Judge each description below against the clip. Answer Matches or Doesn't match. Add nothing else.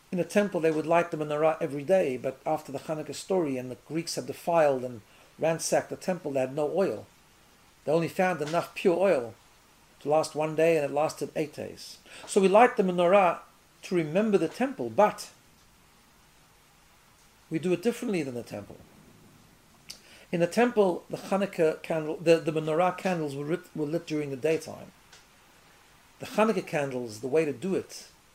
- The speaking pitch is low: Doesn't match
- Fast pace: Doesn't match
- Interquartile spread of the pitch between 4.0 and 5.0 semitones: Doesn't match